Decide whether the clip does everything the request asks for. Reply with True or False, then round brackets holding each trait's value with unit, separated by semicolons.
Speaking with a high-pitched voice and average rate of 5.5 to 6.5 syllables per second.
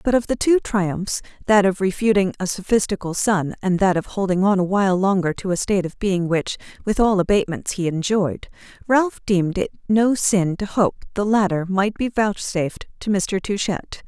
False (195 Hz; 5.1 syllables/s)